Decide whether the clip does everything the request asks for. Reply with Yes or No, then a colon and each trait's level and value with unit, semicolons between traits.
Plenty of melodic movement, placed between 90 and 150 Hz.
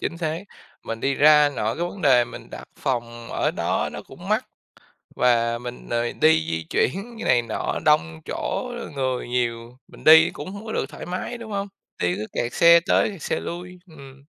Yes: wide, 6.3 semitones; medium, 140 Hz